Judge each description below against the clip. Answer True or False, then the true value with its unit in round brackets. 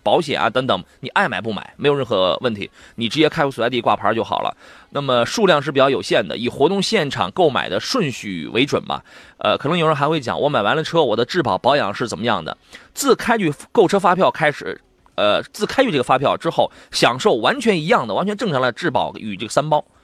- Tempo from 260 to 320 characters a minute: False (340 characters per minute)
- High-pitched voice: False (145 Hz)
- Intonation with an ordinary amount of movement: True (4.7 semitones)